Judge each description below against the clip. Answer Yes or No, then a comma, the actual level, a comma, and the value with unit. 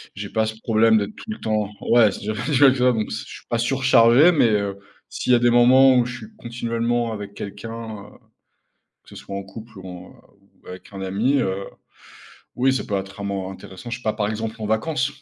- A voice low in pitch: Yes, low, 110 Hz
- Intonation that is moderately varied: Yes, average, 3.1 semitones